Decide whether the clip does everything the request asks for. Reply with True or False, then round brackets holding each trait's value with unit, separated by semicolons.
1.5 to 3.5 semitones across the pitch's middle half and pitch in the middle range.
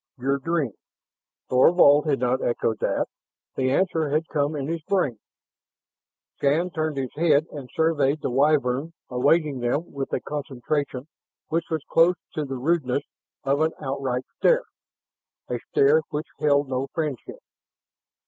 True (3.2 semitones; 145 Hz)